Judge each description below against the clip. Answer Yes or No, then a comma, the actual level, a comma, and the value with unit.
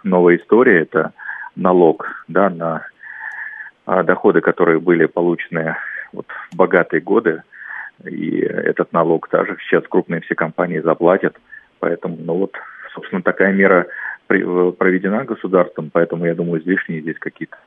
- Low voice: Yes, very low, 85 Hz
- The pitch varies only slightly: Yes, narrow, 1.8 semitones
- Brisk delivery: No, average, 125 wpm